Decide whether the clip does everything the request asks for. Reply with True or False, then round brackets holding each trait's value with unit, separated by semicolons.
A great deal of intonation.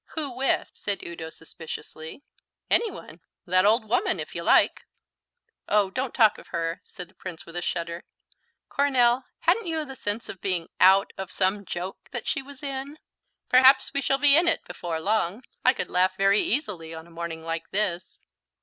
True (7.5 semitones)